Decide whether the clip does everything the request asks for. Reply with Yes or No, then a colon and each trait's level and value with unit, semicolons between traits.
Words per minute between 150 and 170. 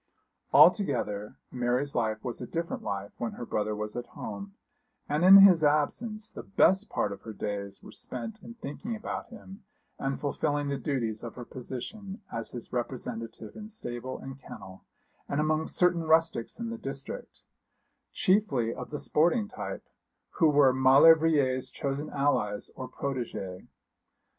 Yes: average, 155 wpm